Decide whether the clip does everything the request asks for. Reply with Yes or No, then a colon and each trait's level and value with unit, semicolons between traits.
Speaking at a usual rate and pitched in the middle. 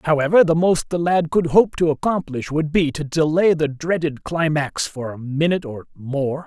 Yes: average, 195 wpm; medium, 155 Hz